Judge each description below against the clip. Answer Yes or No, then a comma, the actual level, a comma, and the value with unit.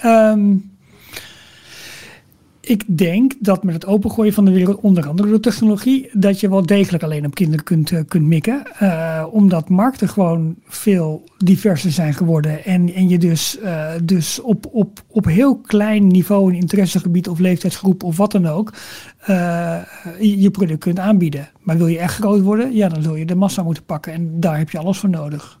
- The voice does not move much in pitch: No, average, 3.4 semitones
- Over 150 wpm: Yes, average, 185 wpm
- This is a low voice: No, medium, 185 Hz